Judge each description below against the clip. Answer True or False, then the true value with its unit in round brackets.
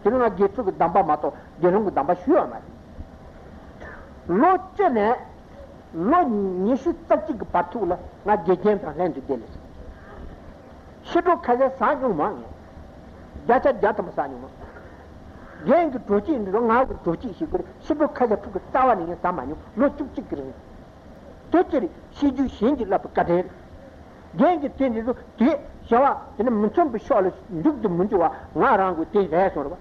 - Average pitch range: False (7.5 semitones)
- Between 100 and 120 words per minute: True (115 wpm)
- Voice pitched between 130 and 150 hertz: False (240 Hz)